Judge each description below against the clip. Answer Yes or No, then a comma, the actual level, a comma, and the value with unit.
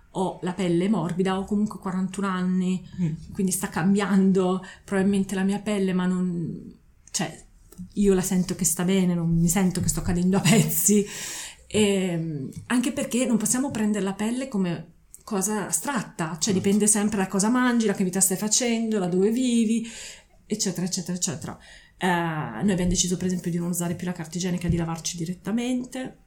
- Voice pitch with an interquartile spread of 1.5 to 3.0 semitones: Yes, narrow, 2.6 semitones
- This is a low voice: No, high, 190 Hz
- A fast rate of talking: Yes, fast, 175 wpm